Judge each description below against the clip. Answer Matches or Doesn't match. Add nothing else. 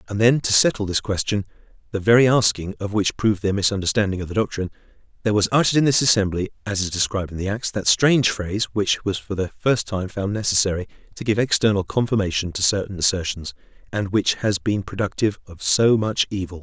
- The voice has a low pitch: Matches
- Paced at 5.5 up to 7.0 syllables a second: Matches